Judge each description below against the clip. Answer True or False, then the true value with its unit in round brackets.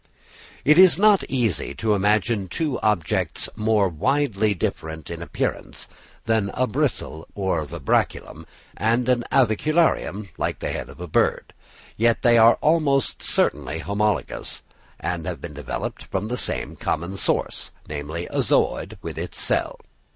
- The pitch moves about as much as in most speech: False (6.3 semitones)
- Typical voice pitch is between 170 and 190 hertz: False (105 Hz)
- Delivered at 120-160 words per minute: True (145 wpm)